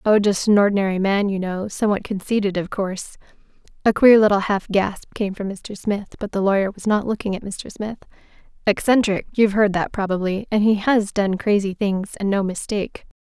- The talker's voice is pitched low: No, high, 200 Hz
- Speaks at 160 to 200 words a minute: Yes, average, 185 wpm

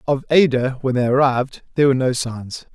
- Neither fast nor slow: Yes, average, 195 wpm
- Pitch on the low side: Yes, low, 130 Hz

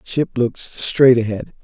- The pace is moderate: Yes, average, 145 wpm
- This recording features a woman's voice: No, male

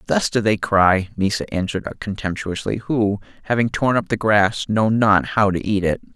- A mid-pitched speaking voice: No, low, 105 Hz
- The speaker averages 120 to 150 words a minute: No, average, 185 wpm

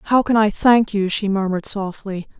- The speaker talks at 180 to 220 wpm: Yes, average, 200 wpm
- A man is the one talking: No, female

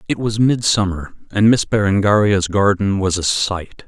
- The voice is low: Yes, low, 100 Hz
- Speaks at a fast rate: No, average, 155 wpm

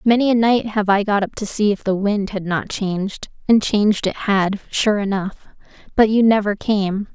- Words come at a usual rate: No, fast, 210 wpm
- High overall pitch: Yes, high, 205 Hz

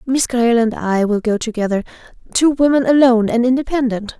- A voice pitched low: No, high, 240 Hz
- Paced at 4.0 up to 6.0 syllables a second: Yes, 5.9 syllables/s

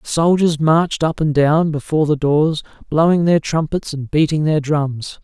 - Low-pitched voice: No, medium, 155 Hz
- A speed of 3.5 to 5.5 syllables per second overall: Yes, 4.5 syllables/s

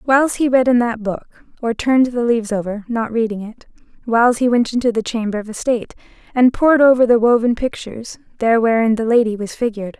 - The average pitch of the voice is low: No, high, 235 Hz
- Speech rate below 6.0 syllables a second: No, 6.2 syllables/s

